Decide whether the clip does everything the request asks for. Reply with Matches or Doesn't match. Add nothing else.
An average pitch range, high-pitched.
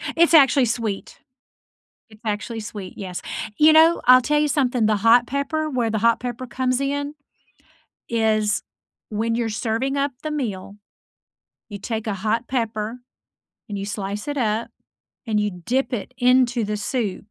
Matches